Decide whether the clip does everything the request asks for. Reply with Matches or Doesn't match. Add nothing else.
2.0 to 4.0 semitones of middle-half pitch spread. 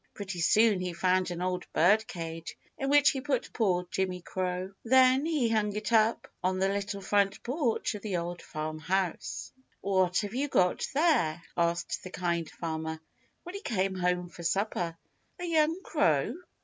Doesn't match